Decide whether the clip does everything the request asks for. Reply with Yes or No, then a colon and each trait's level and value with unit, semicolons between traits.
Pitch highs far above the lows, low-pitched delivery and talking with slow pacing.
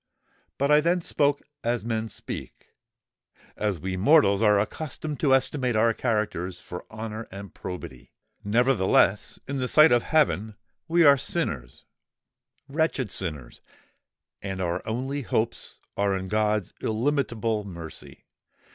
Yes: wide, 5.8 semitones; low, 110 Hz; slow, 120 wpm